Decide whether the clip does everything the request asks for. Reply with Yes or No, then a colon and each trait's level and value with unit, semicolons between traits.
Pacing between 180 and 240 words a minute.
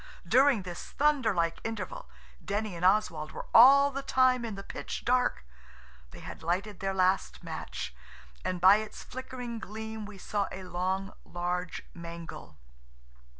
No: average, 150 wpm